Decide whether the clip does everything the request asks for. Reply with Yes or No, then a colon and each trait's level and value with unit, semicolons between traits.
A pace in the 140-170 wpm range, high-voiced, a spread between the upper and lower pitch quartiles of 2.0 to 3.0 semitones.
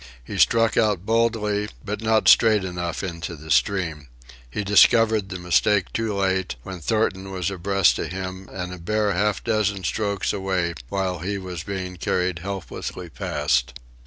No: average, 160 wpm; very low, 95 Hz; average, 2.7 semitones